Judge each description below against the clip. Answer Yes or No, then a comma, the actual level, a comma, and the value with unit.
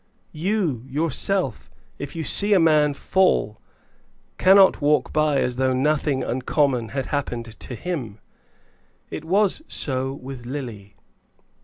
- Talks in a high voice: No, medium, 140 Hz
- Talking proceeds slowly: Yes, slow, 125 wpm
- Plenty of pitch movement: No, average, 4.2 semitones